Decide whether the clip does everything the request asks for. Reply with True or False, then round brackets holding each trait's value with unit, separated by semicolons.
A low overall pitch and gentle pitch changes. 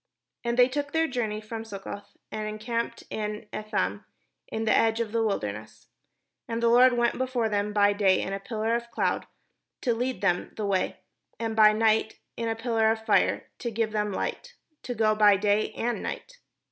False (220 Hz; 2.1 semitones)